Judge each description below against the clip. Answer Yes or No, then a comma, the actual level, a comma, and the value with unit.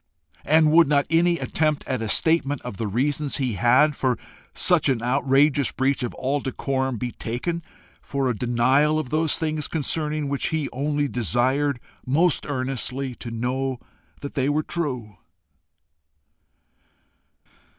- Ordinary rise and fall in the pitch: Yes, average, 3.3 semitones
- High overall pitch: No, low, 135 Hz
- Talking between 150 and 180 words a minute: No, average, 140 wpm